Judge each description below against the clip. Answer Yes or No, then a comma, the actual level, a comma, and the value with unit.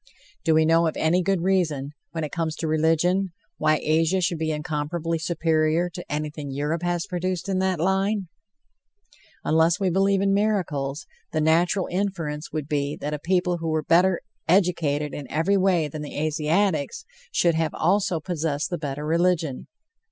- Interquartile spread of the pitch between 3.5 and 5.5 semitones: No, average, 3.0 semitones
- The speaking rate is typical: Yes, average, 165 wpm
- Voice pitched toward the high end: No, medium, 165 Hz